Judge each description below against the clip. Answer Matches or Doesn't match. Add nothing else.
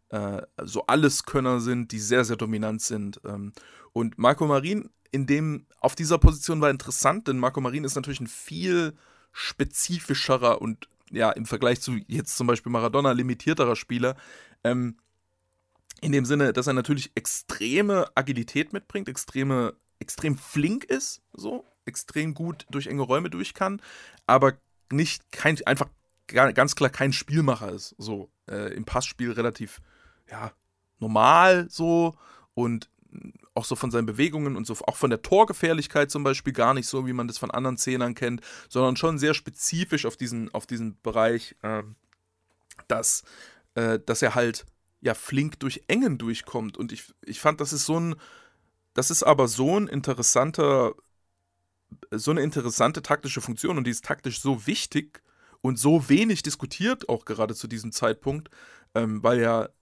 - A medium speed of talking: Matches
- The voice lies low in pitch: Matches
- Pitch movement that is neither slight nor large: Matches